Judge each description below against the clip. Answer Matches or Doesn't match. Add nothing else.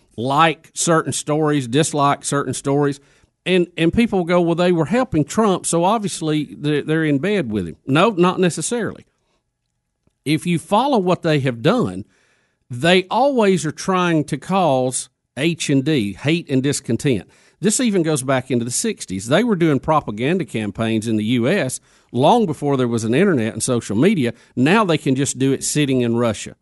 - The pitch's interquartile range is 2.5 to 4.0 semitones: Doesn't match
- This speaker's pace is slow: Doesn't match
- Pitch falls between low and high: Matches